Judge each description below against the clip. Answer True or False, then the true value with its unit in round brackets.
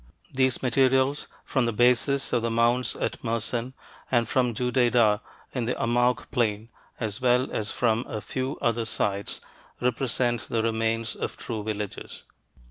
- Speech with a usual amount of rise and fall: False (1.9 semitones)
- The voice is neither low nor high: False (120 Hz)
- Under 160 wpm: True (145 wpm)